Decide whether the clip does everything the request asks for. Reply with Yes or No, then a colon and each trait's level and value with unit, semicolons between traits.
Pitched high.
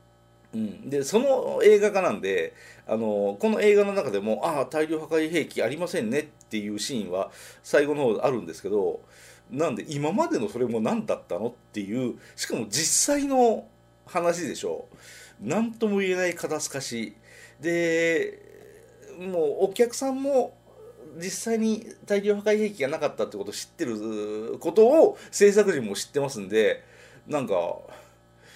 Yes: high, 205 Hz